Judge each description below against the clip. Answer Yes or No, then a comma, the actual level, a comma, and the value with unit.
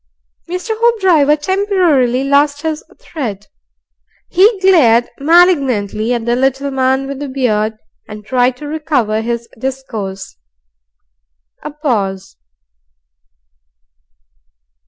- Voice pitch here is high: Yes, very high, 270 Hz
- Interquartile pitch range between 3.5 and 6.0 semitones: Yes, average, 5.1 semitones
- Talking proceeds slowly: Yes, slow, 95 wpm